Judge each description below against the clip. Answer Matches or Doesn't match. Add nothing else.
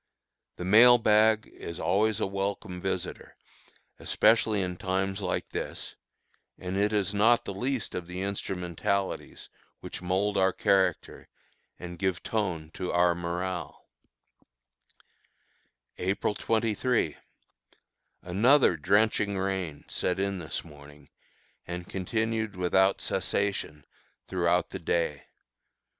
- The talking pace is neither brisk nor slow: Doesn't match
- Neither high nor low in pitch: Doesn't match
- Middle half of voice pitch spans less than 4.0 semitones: Matches